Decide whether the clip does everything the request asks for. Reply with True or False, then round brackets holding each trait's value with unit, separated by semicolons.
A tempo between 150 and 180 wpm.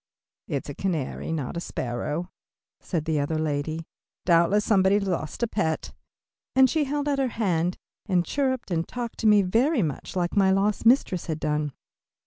True (165 wpm)